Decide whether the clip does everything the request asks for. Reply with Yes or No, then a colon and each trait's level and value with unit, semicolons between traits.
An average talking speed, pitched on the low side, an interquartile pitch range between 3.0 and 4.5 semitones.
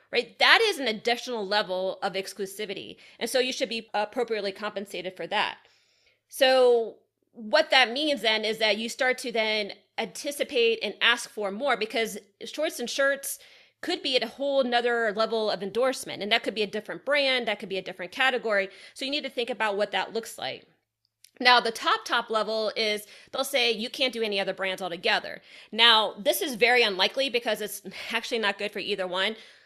No: average, 195 wpm; high, 225 Hz; average, 3.8 semitones